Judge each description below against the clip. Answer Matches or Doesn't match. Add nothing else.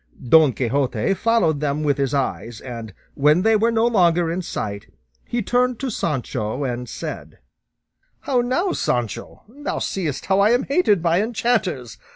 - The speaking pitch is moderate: Matches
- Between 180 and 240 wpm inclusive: Doesn't match